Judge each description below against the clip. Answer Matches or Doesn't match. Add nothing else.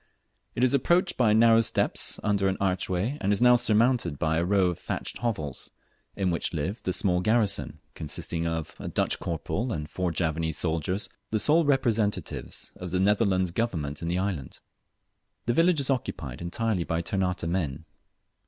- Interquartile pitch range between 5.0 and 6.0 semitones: Matches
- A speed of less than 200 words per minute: Matches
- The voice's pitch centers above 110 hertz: Doesn't match